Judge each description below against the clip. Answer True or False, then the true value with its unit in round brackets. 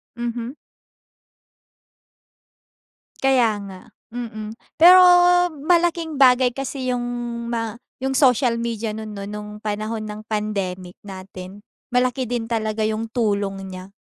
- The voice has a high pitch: True (225 Hz)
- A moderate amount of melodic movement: True (3.1 semitones)